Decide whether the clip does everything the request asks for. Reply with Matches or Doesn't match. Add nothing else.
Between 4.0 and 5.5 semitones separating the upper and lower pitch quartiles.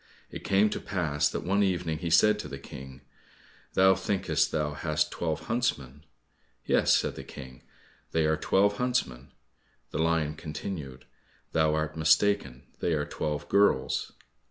Matches